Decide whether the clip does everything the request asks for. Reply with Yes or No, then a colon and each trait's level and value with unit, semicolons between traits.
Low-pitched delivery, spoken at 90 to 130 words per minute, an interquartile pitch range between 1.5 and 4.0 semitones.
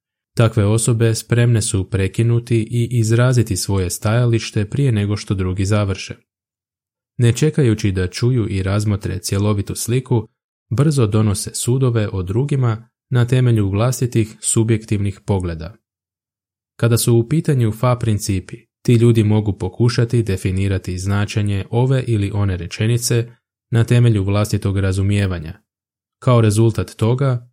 Yes: low, 110 Hz; average, 120 wpm; average, 3.0 semitones